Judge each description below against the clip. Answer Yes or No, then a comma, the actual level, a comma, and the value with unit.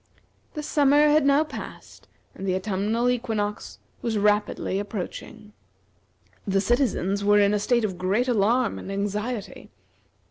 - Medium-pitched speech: No, high, 210 Hz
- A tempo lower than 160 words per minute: Yes, slow, 135 wpm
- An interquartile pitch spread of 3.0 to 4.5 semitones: Yes, average, 3.7 semitones